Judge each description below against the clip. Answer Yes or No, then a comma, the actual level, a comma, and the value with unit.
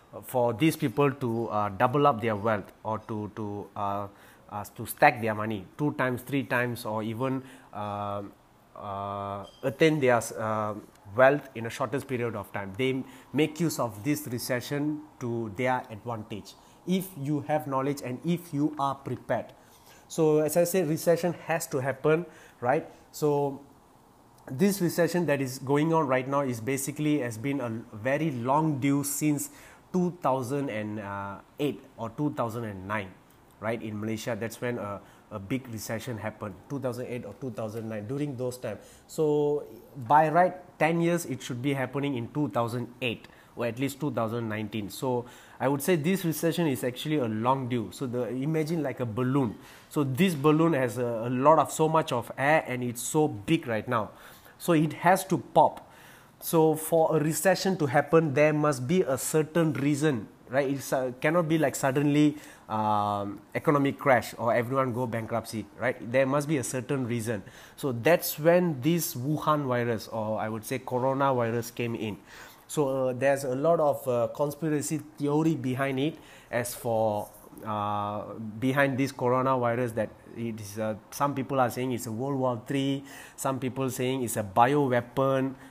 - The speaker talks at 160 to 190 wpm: Yes, average, 165 wpm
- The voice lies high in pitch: No, low, 130 Hz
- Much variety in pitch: No, average, 4.3 semitones